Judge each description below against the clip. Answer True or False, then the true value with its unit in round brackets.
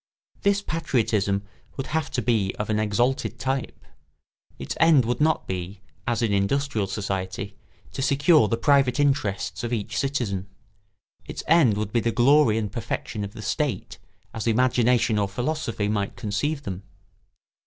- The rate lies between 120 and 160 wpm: True (155 wpm)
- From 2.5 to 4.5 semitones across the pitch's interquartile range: False (5.1 semitones)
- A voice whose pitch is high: False (115 Hz)